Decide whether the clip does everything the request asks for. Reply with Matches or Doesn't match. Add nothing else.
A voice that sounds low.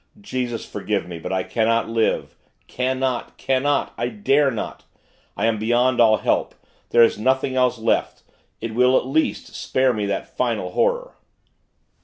Matches